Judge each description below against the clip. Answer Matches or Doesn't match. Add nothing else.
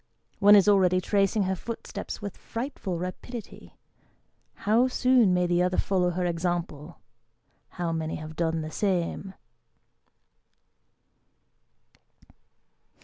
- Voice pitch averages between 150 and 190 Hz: Matches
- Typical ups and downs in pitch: Matches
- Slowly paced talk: Matches